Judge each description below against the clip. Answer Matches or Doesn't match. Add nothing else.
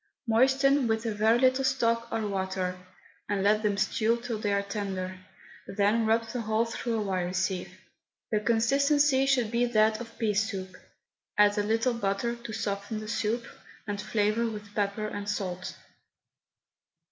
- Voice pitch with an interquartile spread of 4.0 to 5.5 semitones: Doesn't match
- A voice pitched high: Matches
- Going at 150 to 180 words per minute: Matches